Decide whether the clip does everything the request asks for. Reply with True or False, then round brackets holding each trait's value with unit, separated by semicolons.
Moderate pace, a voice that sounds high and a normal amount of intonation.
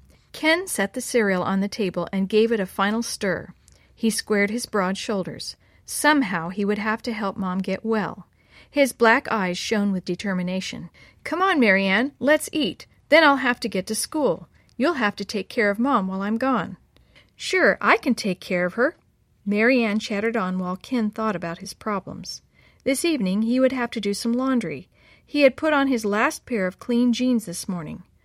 True (195 wpm; 220 Hz; 4.5 semitones)